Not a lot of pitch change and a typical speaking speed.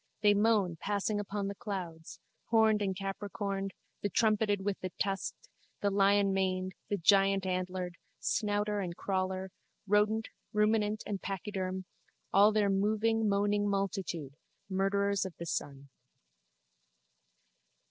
No: narrow, 1.7 semitones; slow, 115 wpm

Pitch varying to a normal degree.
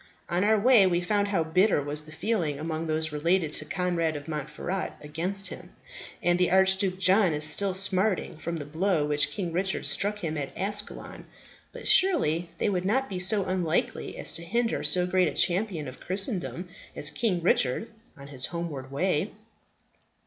Yes: average, 3.8 semitones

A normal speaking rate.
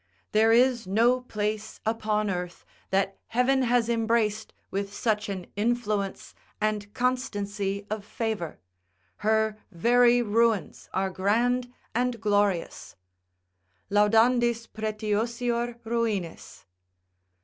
No: slow, 95 wpm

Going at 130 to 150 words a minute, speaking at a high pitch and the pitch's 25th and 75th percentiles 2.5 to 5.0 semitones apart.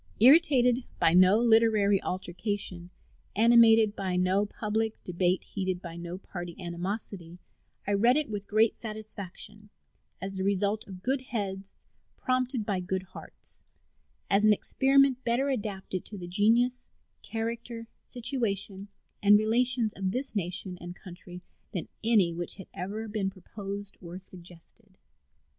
Yes: slow, 135 wpm; high, 205 Hz; average, 3.4 semitones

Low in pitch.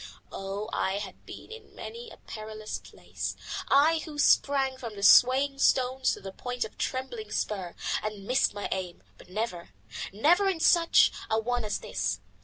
No: high, 225 Hz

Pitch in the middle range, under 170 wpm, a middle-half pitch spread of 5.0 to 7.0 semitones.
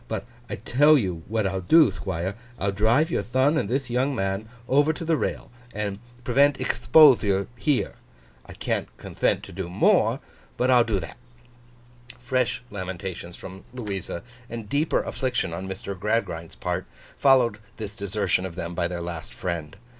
No: low, 105 Hz; average, 160 wpm; wide, 5.5 semitones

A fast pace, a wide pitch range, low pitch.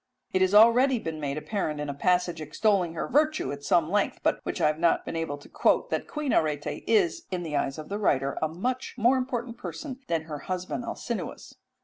No: fast, 220 wpm; wide, 7.5 semitones; medium, 180 Hz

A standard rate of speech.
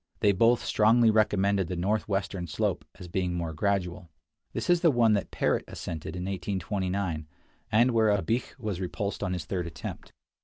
Yes: average, 170 wpm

